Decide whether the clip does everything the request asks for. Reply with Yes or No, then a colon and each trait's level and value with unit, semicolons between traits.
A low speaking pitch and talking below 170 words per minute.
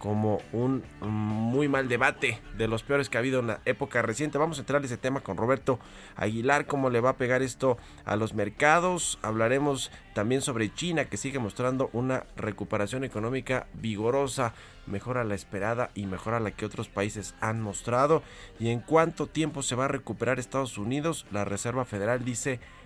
No: low, 120 Hz; fast, 190 wpm